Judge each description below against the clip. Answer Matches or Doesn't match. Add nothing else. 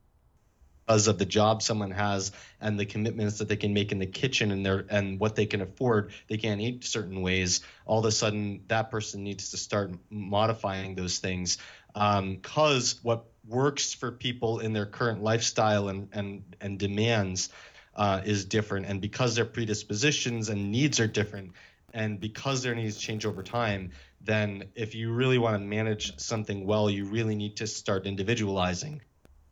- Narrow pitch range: Matches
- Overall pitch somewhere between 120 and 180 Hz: Doesn't match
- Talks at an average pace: Matches